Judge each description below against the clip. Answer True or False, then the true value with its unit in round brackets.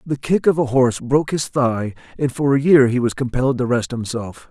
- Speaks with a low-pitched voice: True (130 Hz)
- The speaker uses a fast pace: True (240 wpm)